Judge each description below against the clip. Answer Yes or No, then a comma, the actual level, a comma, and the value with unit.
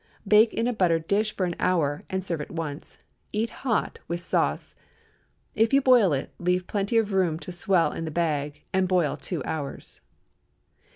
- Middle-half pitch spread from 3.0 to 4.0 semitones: No, average, 4.4 semitones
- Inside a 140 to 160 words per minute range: No, average, 180 wpm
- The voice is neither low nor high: Yes, medium, 180 Hz